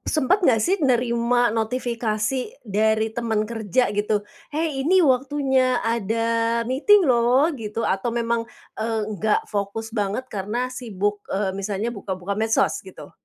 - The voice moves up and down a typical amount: Yes, average, 3.1 semitones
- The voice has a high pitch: Yes, high, 230 Hz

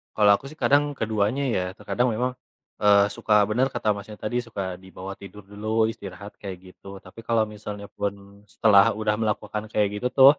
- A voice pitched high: No, low, 105 Hz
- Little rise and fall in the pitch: Yes, narrow, 1.8 semitones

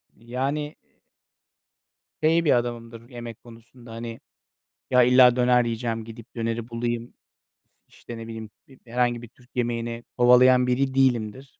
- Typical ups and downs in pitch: No, narrow, 1.5 semitones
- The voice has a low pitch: Yes, low, 120 Hz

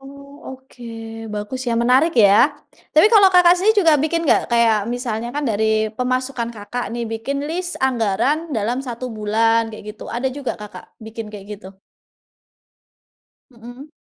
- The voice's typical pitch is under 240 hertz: No, high, 245 Hz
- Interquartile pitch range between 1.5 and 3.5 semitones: No, average, 3.9 semitones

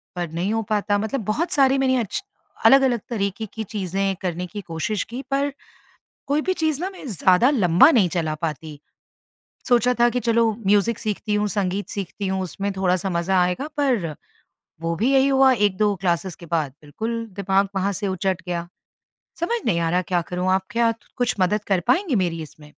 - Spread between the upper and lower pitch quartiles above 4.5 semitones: Yes, average, 5.0 semitones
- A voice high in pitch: Yes, high, 200 Hz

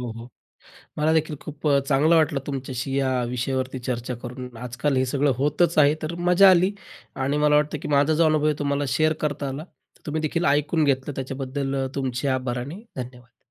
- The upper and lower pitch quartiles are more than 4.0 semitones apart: No, average, 2.7 semitones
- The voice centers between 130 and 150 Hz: Yes, medium, 140 Hz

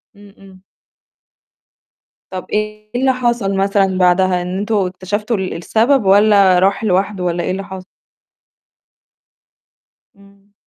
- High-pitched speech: Yes, high, 195 Hz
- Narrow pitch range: Yes, narrow, 2.1 semitones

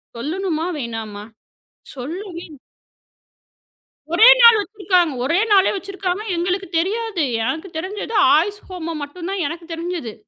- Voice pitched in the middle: No, very high, 350 Hz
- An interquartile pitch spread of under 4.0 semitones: Yes, average, 3.6 semitones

